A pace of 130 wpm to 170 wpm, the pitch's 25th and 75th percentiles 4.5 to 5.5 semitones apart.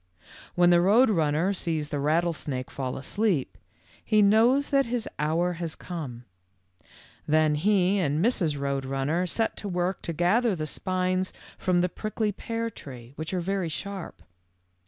Yes: average, 155 wpm; average, 4.9 semitones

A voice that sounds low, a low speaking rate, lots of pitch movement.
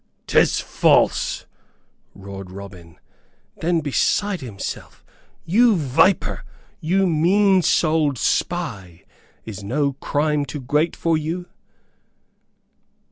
No: medium, 150 Hz; slow, 90 wpm; wide, 8.0 semitones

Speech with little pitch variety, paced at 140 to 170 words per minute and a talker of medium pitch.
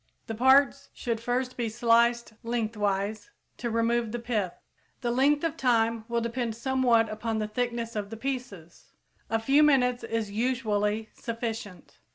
No: narrow, 2.1 semitones; average, 150 wpm; high, 230 Hz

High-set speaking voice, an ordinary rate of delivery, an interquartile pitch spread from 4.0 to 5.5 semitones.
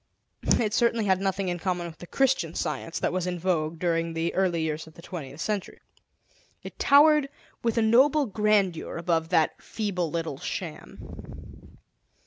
No: medium, 180 Hz; average, 160 wpm; average, 4.3 semitones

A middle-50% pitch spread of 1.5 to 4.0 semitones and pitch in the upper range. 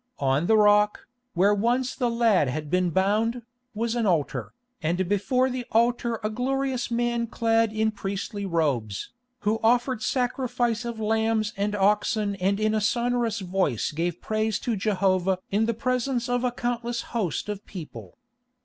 Yes: average, 3.5 semitones; high, 220 Hz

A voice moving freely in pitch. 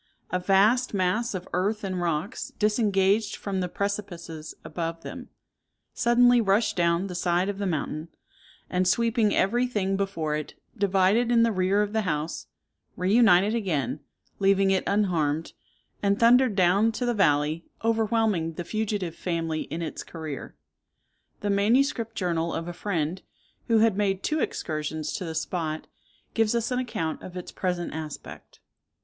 No: average, 4.3 semitones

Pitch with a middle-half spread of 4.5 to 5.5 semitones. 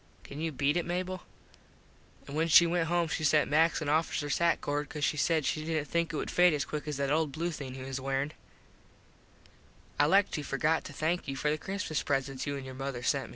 No: average, 2.9 semitones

